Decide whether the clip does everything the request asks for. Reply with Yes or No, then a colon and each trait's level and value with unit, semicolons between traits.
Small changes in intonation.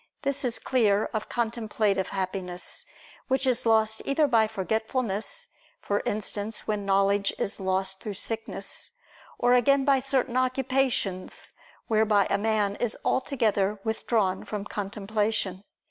No: average, 3.7 semitones